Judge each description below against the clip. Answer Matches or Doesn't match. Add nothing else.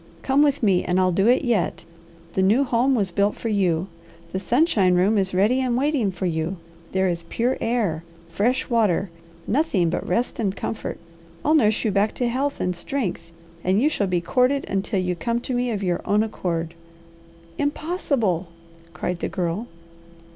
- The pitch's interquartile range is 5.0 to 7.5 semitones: Matches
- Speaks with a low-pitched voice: Doesn't match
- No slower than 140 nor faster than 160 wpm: Doesn't match